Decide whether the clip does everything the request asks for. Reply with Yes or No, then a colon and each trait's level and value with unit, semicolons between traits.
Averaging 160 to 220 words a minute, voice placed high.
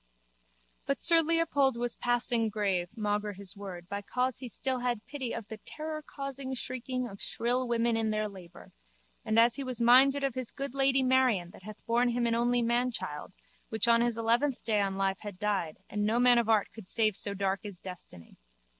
Yes: average, 200 wpm; high, 235 Hz